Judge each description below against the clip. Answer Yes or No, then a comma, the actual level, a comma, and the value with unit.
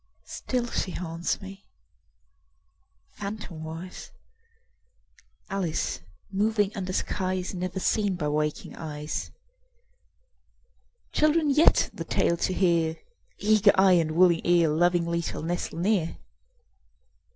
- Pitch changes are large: No, average, 3.2 semitones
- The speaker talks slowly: Yes, slow, 100 wpm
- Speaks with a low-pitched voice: No, medium, 180 Hz